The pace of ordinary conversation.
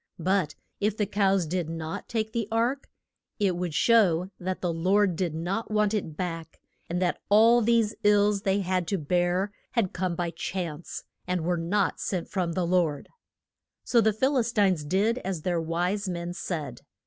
Yes: average, 180 wpm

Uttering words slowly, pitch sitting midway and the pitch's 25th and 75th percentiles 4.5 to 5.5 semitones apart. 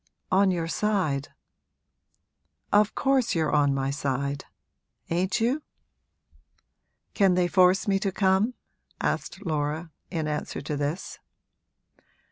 Yes: slow, 110 wpm; medium, 180 Hz; average, 5.0 semitones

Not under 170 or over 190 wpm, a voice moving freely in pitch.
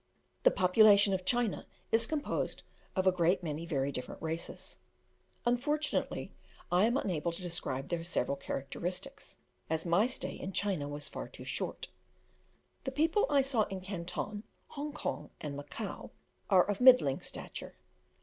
No: average, 150 wpm; wide, 6.4 semitones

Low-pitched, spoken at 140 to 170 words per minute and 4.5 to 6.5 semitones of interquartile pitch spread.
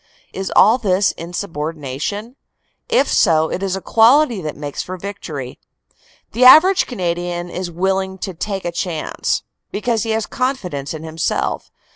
No: high, 190 Hz; average, 150 wpm; average, 5.0 semitones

